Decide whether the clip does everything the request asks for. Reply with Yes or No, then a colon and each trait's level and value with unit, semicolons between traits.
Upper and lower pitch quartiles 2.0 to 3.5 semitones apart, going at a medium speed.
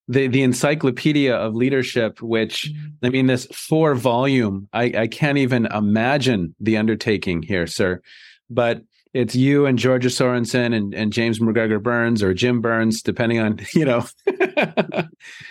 Yes: average, 2.9 semitones; average, 145 wpm